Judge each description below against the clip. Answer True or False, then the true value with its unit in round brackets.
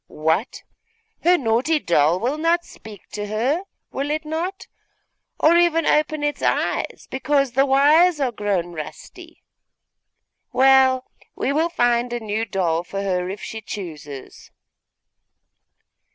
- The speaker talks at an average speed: False (130 wpm)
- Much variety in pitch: True (7.4 semitones)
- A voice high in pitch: True (255 Hz)